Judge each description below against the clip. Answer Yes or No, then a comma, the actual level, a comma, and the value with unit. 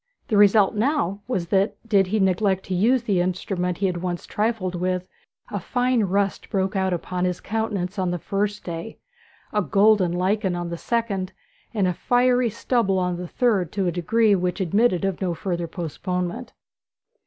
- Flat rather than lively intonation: No, average, 3.0 semitones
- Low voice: No, high, 190 Hz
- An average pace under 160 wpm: No, average, 175 wpm